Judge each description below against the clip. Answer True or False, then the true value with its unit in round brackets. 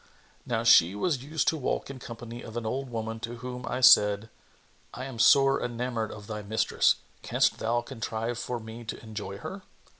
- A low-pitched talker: True (115 Hz)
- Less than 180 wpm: False (185 wpm)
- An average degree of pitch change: False (2.3 semitones)